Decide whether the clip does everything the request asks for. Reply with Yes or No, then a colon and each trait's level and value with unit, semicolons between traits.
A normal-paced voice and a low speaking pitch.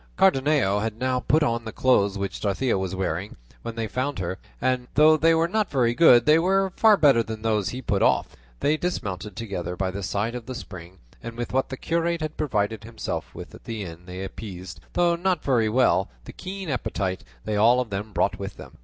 No: fast, 215 wpm; low, 115 Hz